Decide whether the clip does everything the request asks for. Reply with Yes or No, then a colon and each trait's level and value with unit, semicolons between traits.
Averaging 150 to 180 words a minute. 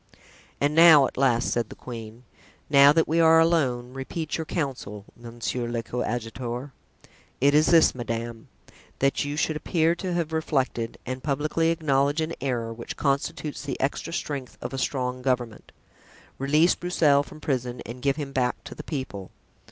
Yes: average, 165 wpm